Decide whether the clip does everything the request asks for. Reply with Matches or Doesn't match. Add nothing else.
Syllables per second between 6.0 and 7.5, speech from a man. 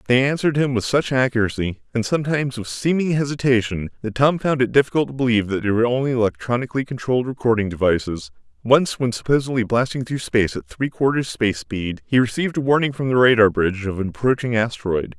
Matches